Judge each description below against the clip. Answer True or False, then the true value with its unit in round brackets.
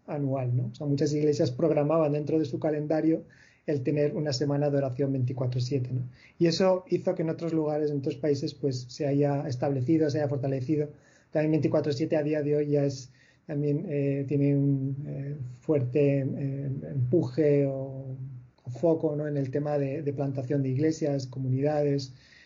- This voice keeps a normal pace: True (175 wpm)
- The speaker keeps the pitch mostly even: True (2.0 semitones)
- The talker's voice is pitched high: False (145 Hz)